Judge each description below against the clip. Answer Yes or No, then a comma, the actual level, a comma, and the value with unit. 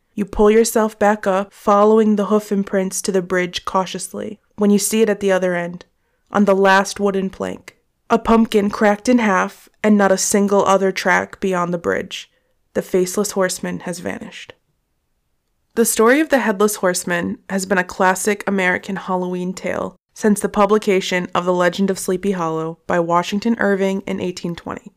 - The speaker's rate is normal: Yes, average, 175 wpm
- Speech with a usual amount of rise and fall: No, narrow, 2.3 semitones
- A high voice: Yes, high, 195 Hz